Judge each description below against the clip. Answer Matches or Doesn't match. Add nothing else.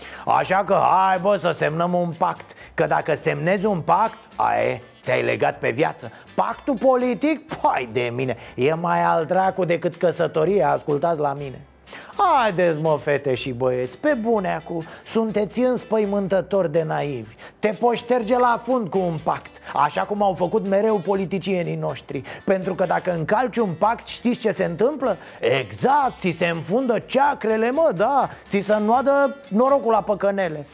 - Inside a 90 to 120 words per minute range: Doesn't match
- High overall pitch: Matches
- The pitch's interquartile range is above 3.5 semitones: Matches